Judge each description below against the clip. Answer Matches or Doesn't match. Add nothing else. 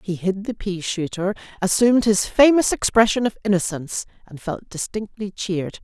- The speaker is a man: Doesn't match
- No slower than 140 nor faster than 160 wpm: Matches